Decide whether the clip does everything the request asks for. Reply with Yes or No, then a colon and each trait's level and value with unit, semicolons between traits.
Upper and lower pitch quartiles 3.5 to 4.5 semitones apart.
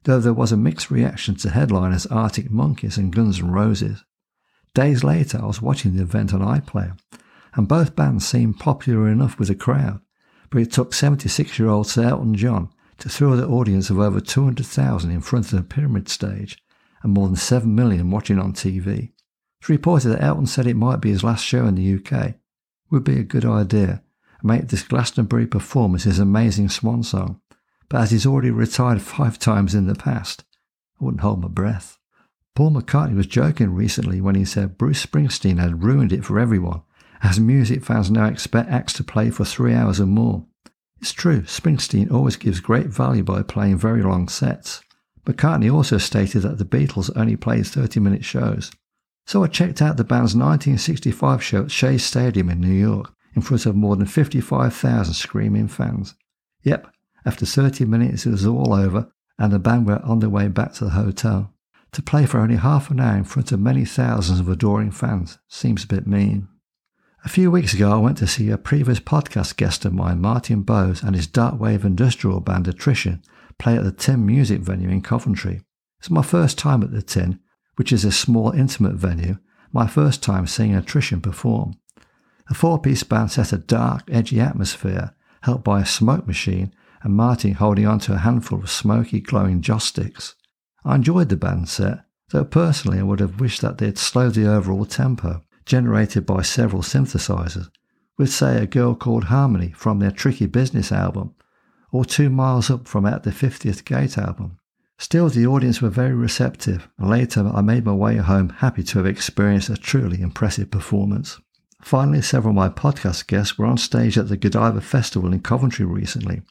Yes: average, 4.2 semitones